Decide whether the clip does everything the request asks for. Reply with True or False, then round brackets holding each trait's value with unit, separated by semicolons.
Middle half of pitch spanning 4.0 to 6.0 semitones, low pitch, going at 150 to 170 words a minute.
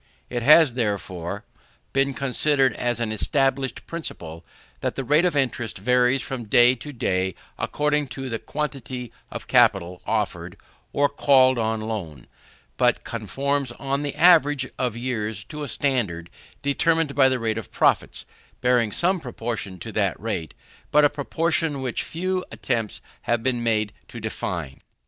True (4.3 semitones; 125 Hz; 155 wpm)